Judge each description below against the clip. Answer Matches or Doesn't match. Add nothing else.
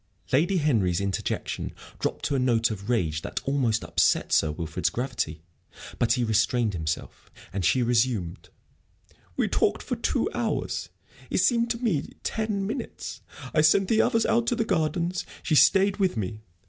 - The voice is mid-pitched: Doesn't match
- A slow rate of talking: Doesn't match